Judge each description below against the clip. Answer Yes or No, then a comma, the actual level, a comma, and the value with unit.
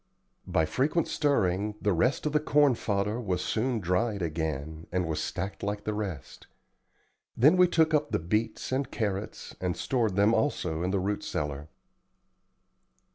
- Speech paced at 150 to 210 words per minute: Yes, average, 160 wpm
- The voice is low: Yes, low, 105 Hz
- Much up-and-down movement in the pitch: Yes, wide, 6.1 semitones